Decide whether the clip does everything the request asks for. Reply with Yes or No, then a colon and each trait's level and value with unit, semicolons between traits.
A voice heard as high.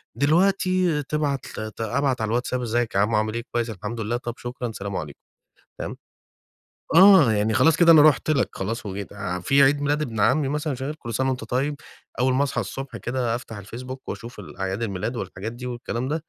No: low, 125 Hz